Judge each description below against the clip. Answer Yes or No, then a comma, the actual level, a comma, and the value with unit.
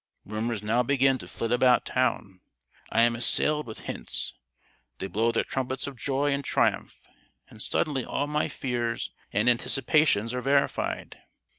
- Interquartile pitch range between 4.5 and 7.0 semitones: No, average, 3.0 semitones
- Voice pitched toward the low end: Yes, low, 125 Hz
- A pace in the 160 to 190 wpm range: No, average, 150 wpm